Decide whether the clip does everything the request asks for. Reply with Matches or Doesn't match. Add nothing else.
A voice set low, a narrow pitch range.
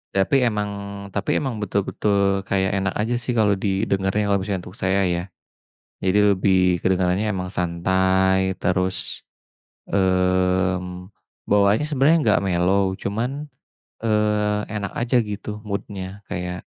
Matches